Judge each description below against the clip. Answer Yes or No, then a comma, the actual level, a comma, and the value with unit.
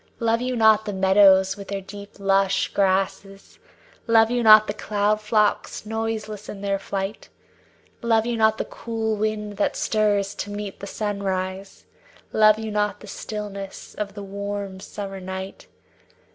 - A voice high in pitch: Yes, high, 205 Hz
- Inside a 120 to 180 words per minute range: Yes, average, 155 wpm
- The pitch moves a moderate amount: No, narrow, 1.7 semitones